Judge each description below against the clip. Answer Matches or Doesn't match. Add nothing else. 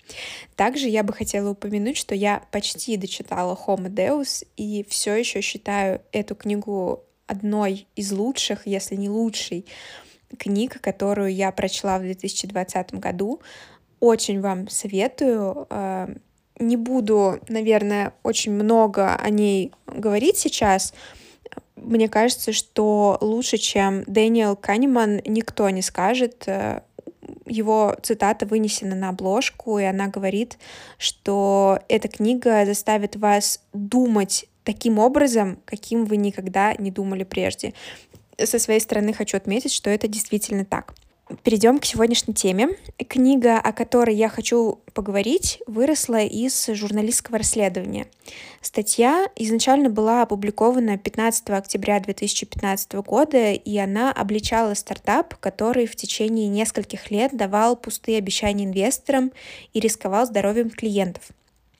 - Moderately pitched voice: Doesn't match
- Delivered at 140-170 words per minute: Doesn't match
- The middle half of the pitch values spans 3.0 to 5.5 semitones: Doesn't match